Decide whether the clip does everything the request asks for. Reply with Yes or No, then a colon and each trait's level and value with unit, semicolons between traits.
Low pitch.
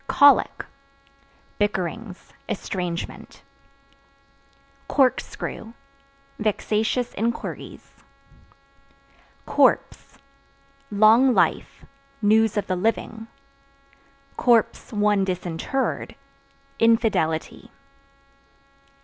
No: high, 215 Hz